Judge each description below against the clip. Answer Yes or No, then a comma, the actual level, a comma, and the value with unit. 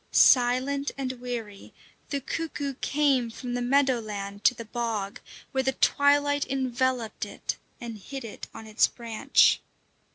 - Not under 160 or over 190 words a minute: No, average, 140 wpm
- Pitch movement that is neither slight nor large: Yes, average, 3.2 semitones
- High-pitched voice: Yes, very high, 250 Hz